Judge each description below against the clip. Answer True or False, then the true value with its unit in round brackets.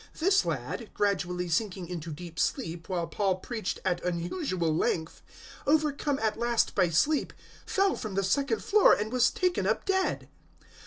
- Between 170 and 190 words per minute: False (155 wpm)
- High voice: True (205 Hz)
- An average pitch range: False (8.1 semitones)